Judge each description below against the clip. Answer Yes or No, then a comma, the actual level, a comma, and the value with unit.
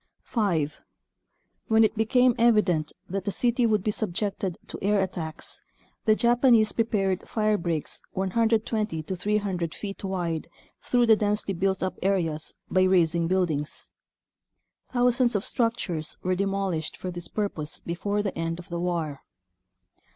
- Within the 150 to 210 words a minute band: No, average, 140 wpm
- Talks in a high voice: Yes, high, 195 Hz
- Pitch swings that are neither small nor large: Yes, average, 4.0 semitones